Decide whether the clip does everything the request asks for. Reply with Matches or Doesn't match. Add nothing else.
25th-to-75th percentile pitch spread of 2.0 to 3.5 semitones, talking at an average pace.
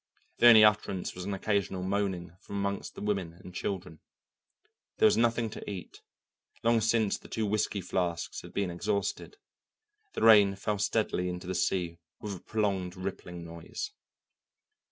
Matches